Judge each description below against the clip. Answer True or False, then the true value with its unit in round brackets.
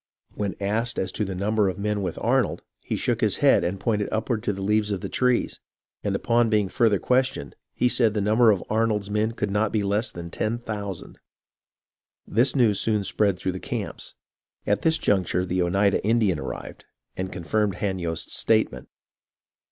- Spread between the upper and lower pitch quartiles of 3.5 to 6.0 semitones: False (2.4 semitones)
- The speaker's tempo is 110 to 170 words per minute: False (185 wpm)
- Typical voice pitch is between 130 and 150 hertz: False (105 Hz)